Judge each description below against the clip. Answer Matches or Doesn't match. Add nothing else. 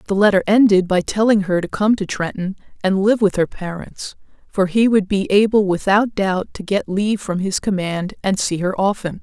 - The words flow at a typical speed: Doesn't match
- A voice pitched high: Matches